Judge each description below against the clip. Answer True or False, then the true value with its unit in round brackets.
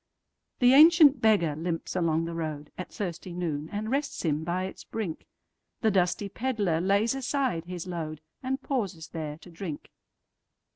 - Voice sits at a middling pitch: True (180 Hz)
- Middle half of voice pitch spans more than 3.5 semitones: True (5.5 semitones)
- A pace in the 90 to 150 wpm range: True (140 wpm)